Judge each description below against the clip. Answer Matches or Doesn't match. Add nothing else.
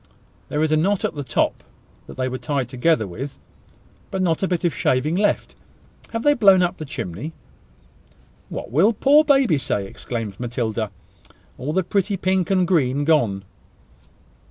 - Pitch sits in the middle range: Matches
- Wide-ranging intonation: Matches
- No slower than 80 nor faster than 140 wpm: Doesn't match